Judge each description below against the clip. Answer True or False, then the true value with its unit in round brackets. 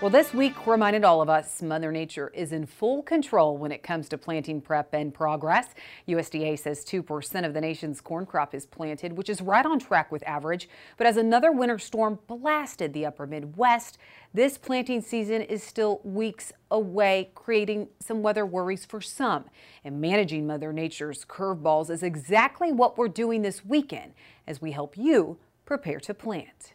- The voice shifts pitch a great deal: True (6.4 semitones)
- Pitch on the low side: False (190 Hz)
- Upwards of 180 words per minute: False (175 wpm)